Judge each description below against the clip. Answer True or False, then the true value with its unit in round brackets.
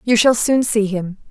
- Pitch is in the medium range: False (220 Hz)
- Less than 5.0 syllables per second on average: True (4.5 syllables/s)